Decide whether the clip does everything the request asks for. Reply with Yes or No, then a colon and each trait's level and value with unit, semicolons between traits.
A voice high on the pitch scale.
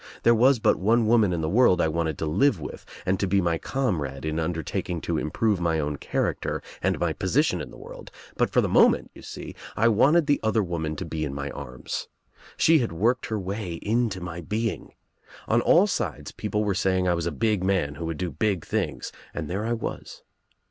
No: very low, 95 Hz